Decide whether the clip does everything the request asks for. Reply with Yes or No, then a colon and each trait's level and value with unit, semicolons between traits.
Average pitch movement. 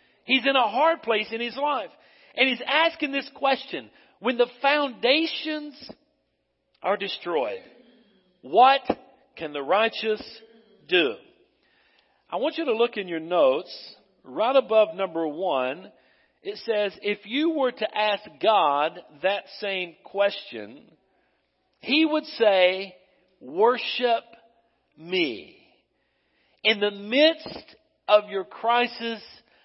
No: wide, 5.9 semitones